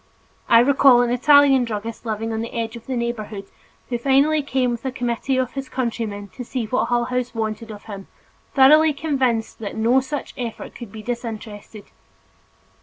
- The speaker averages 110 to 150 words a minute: No, average, 180 wpm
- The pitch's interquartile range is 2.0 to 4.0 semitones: Yes, average, 2.9 semitones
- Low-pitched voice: No, high, 240 Hz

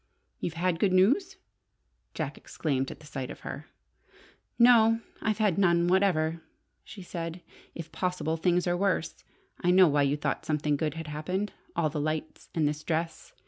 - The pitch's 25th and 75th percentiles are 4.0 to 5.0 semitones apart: No, average, 3.4 semitones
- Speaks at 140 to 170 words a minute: Yes, average, 165 wpm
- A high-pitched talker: No, medium, 170 Hz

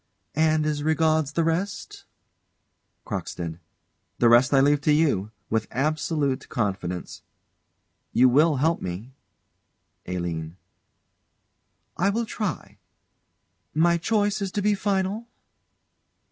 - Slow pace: Yes, slow, 105 wpm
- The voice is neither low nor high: Yes, medium, 150 Hz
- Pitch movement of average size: No, wide, 6.6 semitones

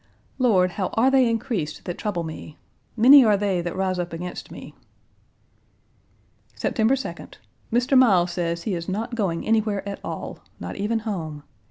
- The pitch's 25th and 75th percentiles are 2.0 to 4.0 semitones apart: No, average, 4.6 semitones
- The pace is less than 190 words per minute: Yes, average, 160 wpm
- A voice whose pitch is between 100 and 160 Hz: No, high, 200 Hz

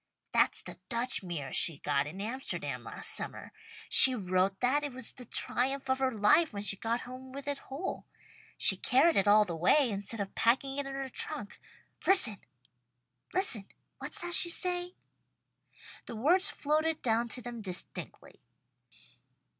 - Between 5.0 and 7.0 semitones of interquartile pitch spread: Yes, wide, 5.6 semitones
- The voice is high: Yes, very high, 250 Hz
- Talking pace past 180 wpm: No, average, 160 wpm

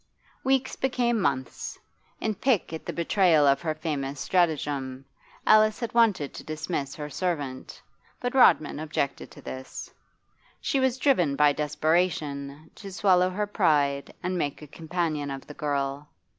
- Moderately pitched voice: Yes, medium, 155 Hz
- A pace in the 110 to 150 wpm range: Yes, average, 145 wpm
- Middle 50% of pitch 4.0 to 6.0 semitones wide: Yes, average, 5.3 semitones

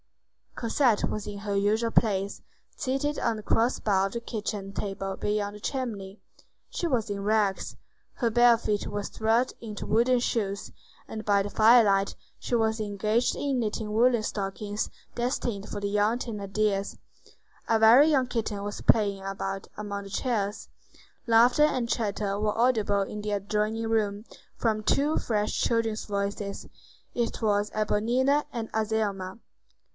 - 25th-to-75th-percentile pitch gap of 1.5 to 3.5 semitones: Yes, narrow, 2.5 semitones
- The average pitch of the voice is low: No, high, 215 Hz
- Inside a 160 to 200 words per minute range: No, average, 150 wpm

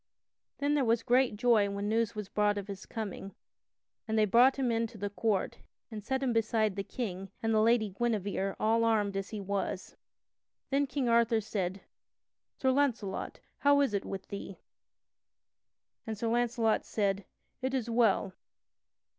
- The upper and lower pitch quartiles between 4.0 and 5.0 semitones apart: No, average, 3.0 semitones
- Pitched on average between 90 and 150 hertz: No, high, 220 Hz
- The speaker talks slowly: No, average, 165 wpm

